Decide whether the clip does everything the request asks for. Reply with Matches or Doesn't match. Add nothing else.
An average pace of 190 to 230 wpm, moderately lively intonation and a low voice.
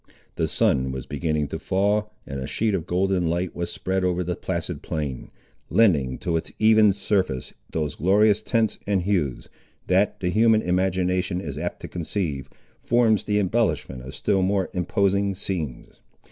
Doesn't match